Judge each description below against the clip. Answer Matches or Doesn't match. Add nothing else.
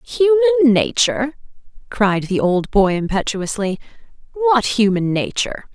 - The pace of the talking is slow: Matches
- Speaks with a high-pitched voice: Matches